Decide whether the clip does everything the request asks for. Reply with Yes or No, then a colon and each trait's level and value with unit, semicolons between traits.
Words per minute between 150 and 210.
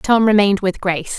Yes: fast, 205 wpm